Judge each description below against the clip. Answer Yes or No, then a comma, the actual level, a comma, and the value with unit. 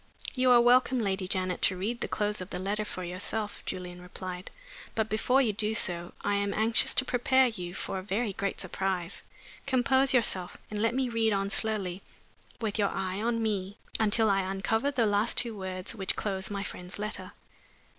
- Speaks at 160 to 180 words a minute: No, average, 190 wpm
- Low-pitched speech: No, high, 205 Hz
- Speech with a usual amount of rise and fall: Yes, average, 3.3 semitones